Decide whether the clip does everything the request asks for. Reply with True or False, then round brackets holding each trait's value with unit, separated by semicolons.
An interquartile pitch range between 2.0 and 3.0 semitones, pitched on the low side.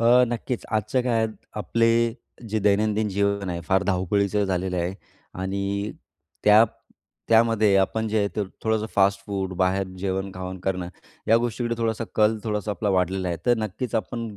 True (2.6 semitones; 100 Hz)